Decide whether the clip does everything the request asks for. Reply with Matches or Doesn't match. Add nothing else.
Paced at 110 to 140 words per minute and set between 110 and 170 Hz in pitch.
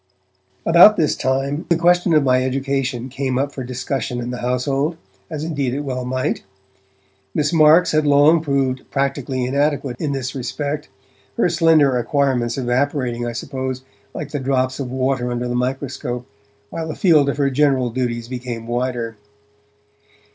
Doesn't match